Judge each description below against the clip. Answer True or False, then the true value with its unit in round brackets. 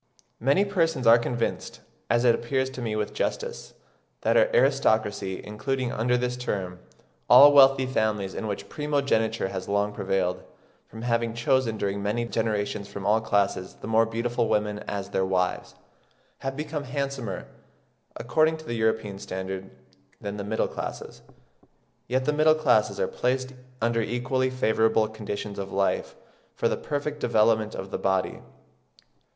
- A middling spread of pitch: True (4.2 semitones)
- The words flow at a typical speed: True (150 wpm)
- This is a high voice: False (115 Hz)